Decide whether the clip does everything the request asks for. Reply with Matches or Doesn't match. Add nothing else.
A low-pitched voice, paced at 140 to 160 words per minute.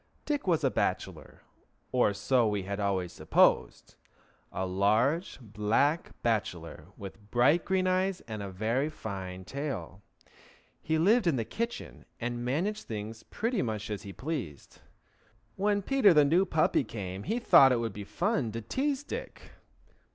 Matches